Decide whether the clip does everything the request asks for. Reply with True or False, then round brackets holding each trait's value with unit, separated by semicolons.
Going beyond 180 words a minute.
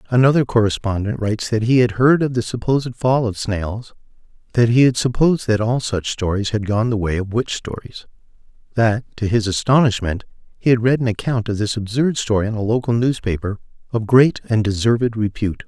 True (190 wpm)